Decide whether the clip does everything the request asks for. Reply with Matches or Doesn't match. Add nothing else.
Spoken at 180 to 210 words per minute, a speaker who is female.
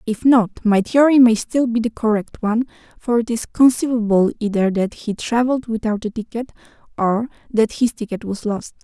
Matches